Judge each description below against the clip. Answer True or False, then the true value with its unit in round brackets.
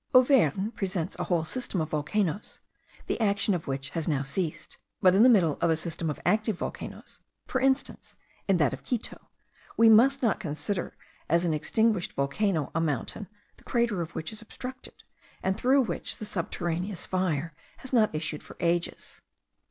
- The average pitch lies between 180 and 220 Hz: True (185 Hz)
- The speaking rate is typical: True (175 wpm)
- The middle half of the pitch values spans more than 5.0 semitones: True (5.5 semitones)